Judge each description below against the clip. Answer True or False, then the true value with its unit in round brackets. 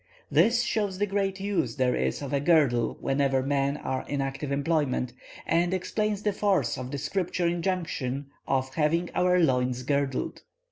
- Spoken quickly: False (160 wpm)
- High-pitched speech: False (145 Hz)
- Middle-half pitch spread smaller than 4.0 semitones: False (5.5 semitones)